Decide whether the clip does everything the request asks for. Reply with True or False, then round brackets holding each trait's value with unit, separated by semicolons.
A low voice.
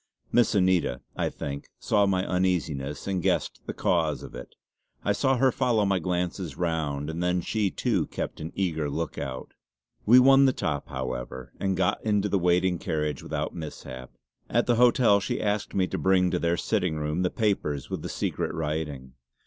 True (90 Hz)